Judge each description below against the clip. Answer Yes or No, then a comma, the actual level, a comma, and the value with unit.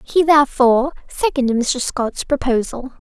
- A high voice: Yes, very high, 265 Hz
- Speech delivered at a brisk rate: No, slow, 115 wpm